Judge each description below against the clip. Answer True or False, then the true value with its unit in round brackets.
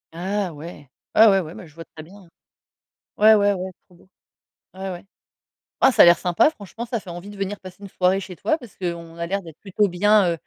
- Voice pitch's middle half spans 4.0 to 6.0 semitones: False (2.9 semitones)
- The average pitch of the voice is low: False (185 Hz)